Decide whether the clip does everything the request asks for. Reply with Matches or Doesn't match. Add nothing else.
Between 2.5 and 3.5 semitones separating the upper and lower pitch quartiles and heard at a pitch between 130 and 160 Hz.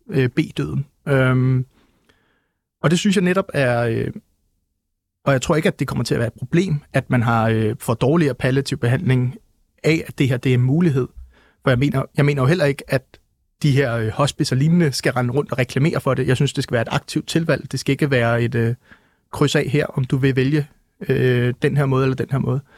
Matches